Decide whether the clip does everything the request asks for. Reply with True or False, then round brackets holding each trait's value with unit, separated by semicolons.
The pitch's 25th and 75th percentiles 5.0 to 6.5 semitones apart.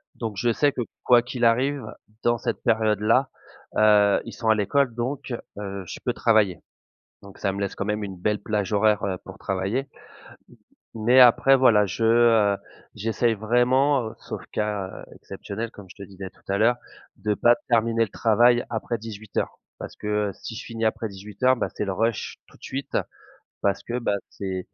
False (2.8 semitones)